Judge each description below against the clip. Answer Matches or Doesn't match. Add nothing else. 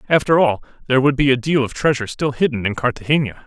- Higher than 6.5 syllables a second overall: Matches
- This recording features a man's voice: Matches